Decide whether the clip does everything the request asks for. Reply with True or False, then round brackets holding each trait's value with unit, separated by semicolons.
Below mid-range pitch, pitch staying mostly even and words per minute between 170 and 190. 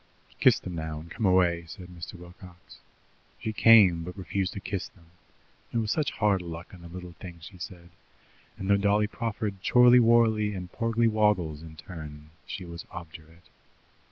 False (90 Hz; 3.7 semitones; 175 wpm)